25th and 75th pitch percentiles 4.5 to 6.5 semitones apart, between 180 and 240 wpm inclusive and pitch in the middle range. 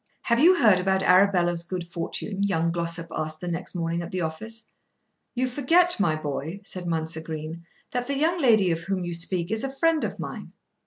Yes: average, 5.3 semitones; average, 200 wpm; medium, 180 Hz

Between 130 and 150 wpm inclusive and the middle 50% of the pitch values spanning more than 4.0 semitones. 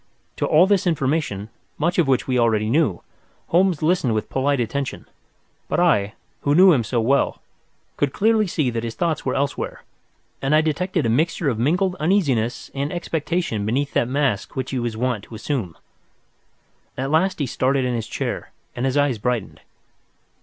No: average, 175 wpm; wide, 5.5 semitones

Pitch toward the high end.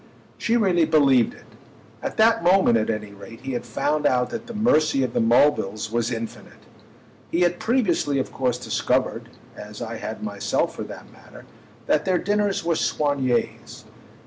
No: medium, 145 Hz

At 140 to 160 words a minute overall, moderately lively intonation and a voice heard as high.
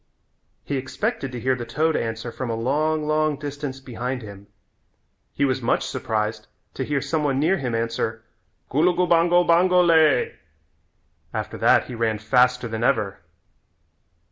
No: average, 145 wpm; average, 5.0 semitones; low, 135 Hz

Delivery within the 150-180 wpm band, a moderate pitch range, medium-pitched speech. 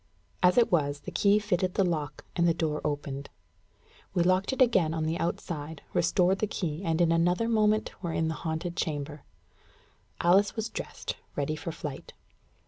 Yes: average, 175 wpm; average, 3.3 semitones; medium, 170 Hz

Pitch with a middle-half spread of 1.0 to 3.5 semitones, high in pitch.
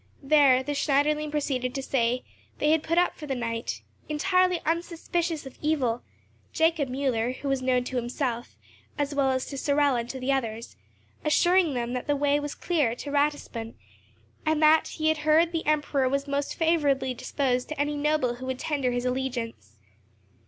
Yes: average, 3.2 semitones; very high, 280 Hz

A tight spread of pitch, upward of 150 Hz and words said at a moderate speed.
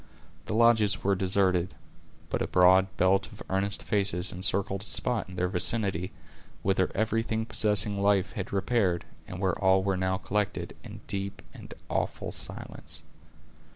No: narrow, 1.9 semitones; very low, 95 Hz; average, 150 wpm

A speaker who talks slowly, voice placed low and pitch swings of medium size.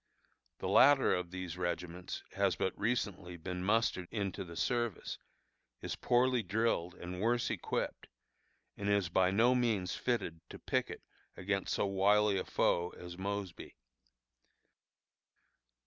Yes: slow, 130 wpm; very low, 95 Hz; average, 3.8 semitones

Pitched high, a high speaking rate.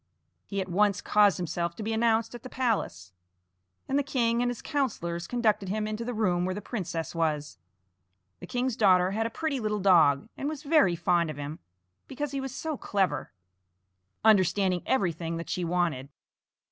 No: high, 205 Hz; average, 180 wpm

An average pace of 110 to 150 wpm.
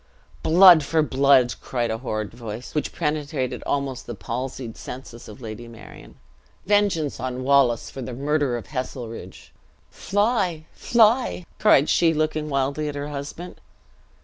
Yes: average, 140 wpm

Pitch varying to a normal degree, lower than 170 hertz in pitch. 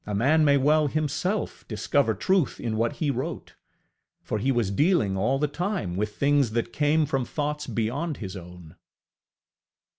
No: wide, 5.7 semitones; low, 135 Hz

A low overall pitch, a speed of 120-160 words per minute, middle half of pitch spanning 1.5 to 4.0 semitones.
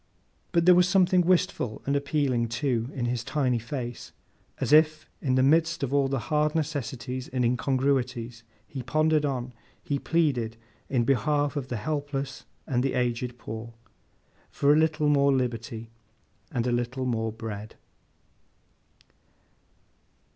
Yes: low, 130 Hz; average, 140 wpm; average, 3.7 semitones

